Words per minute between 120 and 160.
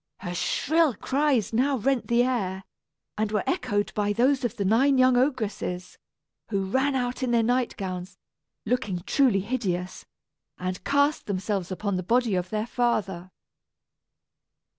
Yes: average, 145 wpm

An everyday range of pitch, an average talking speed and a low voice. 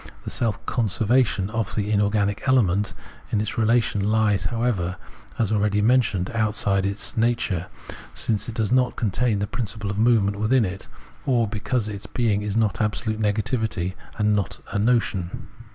No: narrow, 2.3 semitones; average, 160 wpm; low, 105 Hz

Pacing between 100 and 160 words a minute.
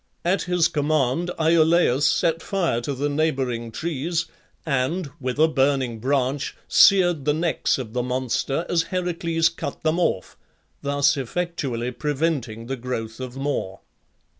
Yes: average, 140 wpm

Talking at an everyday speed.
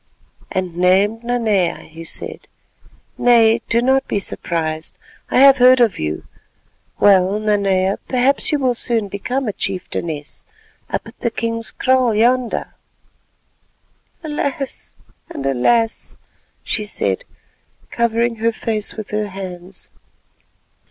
No: slow, 115 wpm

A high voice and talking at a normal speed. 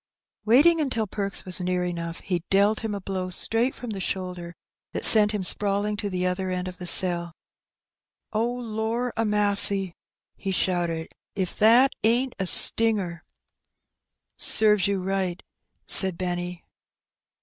Yes: high, 195 Hz; average, 150 wpm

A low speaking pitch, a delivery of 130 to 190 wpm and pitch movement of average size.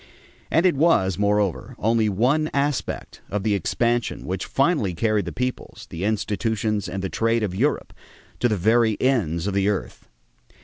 Yes: low, 110 Hz; average, 165 wpm; average, 3.8 semitones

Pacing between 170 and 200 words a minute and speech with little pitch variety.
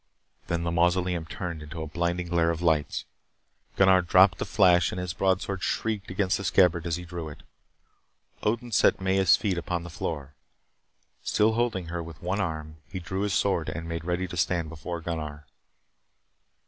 Yes: average, 175 wpm; narrow, 2.2 semitones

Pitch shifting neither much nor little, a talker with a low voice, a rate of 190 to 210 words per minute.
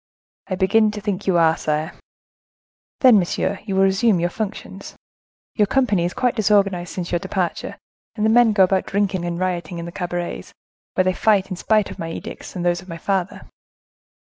No: average, 3.0 semitones; high, 190 Hz; average, 195 wpm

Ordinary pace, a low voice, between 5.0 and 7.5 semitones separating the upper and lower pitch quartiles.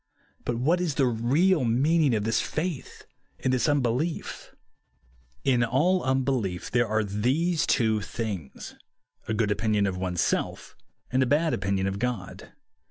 Yes: average, 155 wpm; low, 120 Hz; wide, 5.4 semitones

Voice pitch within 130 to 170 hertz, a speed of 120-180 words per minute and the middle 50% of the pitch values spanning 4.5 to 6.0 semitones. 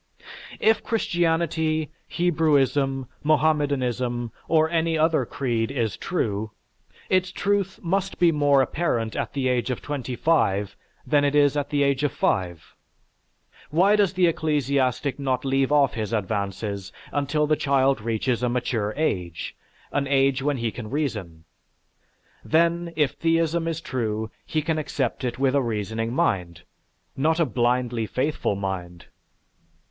Yes: medium, 140 Hz; average, 140 wpm; average, 5.2 semitones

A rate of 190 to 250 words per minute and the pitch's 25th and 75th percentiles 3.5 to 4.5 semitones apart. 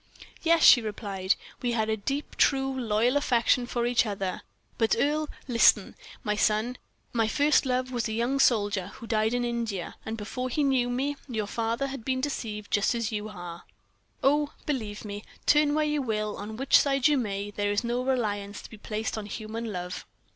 Yes: average, 195 wpm; average, 3.8 semitones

